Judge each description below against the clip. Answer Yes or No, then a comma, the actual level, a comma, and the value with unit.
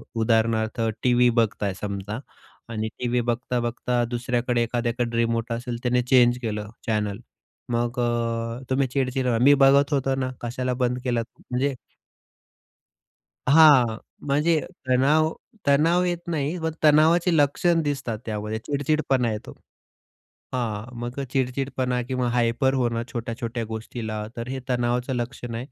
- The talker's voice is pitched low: Yes, low, 125 Hz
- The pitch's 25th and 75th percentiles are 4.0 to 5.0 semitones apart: No, narrow, 2.6 semitones